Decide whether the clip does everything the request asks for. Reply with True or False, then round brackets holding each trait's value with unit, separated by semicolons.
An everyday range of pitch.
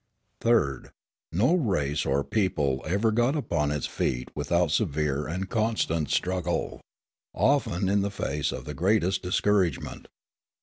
False (5.8 semitones)